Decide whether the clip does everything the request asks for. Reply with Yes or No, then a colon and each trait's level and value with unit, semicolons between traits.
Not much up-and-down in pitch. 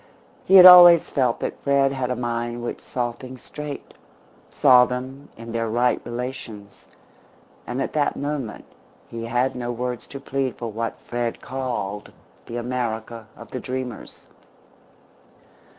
Yes: narrow, 2.3 semitones